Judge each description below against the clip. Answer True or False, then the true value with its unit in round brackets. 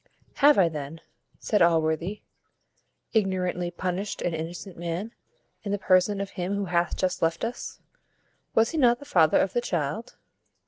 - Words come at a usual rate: True (155 wpm)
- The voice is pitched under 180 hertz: False (185 Hz)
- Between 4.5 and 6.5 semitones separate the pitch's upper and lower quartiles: False (3.4 semitones)